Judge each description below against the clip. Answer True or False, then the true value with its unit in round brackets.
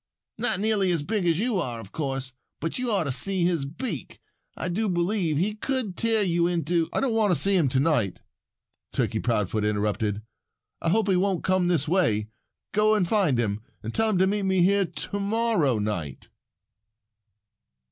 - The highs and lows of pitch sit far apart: True (7.1 semitones)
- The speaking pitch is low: False (175 Hz)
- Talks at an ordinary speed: True (190 wpm)